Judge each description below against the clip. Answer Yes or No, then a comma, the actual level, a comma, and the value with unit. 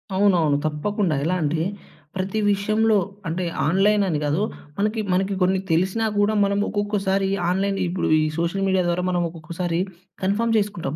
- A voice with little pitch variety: No, average, 3.0 semitones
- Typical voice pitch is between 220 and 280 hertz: No, high, 190 Hz